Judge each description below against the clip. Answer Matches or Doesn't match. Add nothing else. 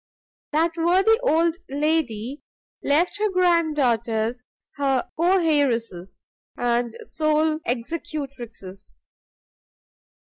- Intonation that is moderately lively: Doesn't match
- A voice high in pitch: Matches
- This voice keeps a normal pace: Doesn't match